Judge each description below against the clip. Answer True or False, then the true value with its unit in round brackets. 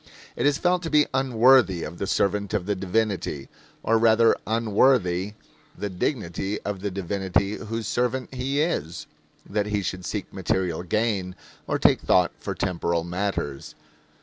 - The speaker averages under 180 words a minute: True (150 wpm)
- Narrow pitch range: False (4.0 semitones)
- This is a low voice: True (100 Hz)